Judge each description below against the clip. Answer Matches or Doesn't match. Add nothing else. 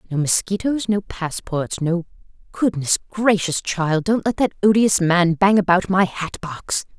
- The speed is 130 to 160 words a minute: Matches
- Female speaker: Matches